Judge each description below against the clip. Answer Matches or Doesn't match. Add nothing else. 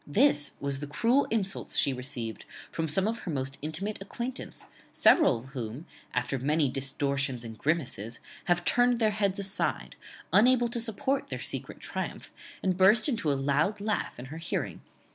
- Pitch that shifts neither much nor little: Doesn't match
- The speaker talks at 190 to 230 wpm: Doesn't match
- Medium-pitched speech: Matches